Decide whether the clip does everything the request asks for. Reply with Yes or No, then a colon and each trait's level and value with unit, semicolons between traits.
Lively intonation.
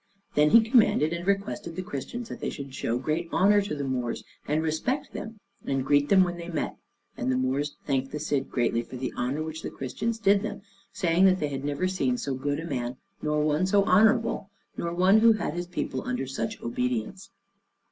Yes: wide, 6.2 semitones